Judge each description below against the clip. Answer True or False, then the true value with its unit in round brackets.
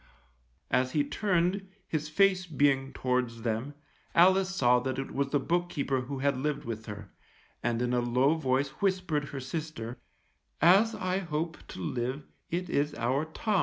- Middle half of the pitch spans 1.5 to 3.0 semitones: False (5.1 semitones)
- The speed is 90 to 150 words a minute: False (165 wpm)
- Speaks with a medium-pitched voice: True (145 Hz)